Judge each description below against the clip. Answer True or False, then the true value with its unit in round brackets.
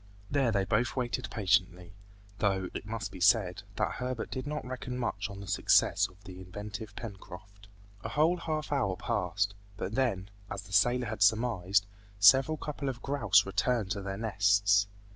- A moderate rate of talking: True (170 wpm)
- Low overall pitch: True (105 Hz)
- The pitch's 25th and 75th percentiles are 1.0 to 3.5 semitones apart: False (4.3 semitones)